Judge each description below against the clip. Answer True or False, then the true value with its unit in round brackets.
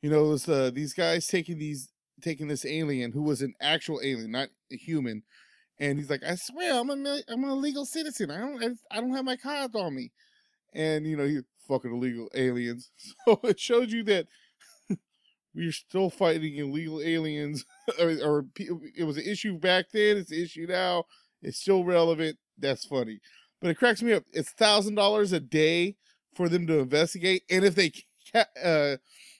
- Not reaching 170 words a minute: False (190 wpm)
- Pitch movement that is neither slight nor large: False (6.1 semitones)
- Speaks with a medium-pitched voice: True (170 Hz)